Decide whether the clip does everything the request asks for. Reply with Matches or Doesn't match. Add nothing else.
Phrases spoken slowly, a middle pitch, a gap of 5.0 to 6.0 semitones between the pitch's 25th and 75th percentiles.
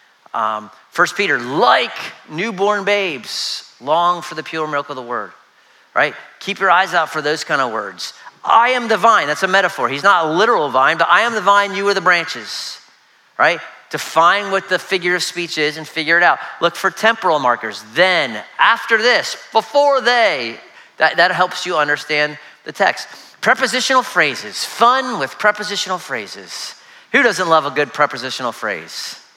Doesn't match